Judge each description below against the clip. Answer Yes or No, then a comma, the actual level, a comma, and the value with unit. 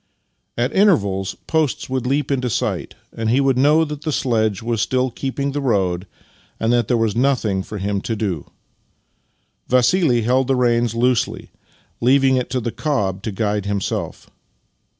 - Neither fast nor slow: Yes, average, 165 wpm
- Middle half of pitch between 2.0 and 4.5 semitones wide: Yes, average, 4.1 semitones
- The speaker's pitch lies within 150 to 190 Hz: No, low, 120 Hz